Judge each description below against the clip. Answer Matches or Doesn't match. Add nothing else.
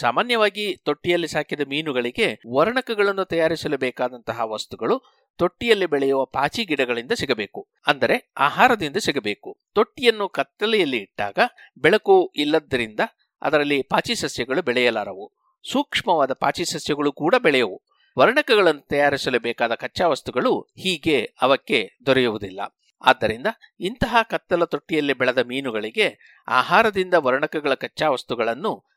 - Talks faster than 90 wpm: Matches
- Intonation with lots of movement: Matches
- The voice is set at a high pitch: Doesn't match